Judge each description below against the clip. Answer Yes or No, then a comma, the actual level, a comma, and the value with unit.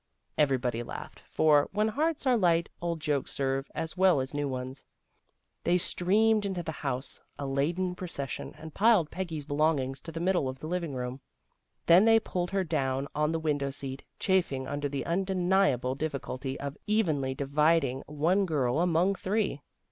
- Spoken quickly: No, average, 170 wpm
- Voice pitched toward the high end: No, medium, 155 Hz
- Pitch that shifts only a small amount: No, average, 4.9 semitones